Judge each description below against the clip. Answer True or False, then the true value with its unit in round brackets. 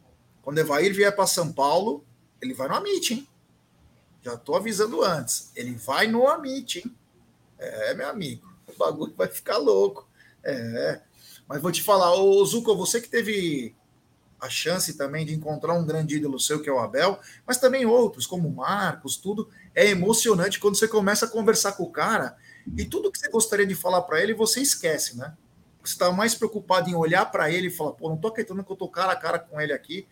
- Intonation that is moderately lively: False (6.3 semitones)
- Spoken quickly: True (205 wpm)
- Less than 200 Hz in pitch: True (190 Hz)